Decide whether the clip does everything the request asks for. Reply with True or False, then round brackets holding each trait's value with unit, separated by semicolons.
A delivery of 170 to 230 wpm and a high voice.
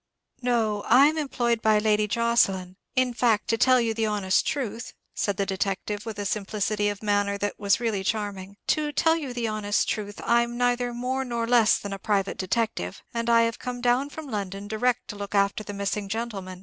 True (200 wpm; 215 Hz)